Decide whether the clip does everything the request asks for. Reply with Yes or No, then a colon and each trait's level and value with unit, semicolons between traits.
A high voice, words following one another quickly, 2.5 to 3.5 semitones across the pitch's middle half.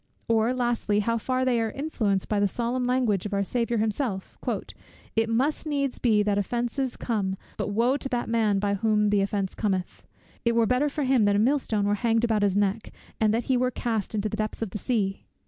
Yes: high, 225 Hz; fast, 220 wpm; average, 3.2 semitones